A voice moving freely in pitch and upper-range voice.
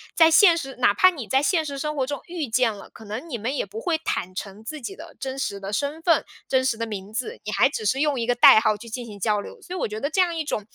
Yes: wide, 6.1 semitones; very high, 260 Hz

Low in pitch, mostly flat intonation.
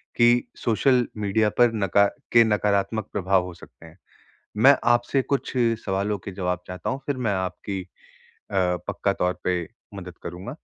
No: low, 100 Hz; average, 4.1 semitones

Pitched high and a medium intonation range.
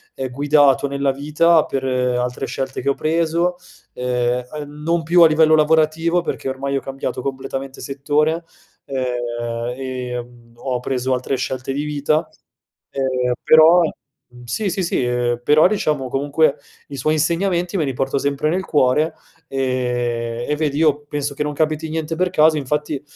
No: medium, 140 Hz; average, 3.5 semitones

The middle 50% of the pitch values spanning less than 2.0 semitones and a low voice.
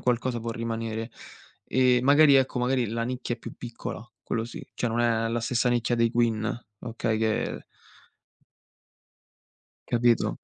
Yes: narrow, 1.5 semitones; low, 120 Hz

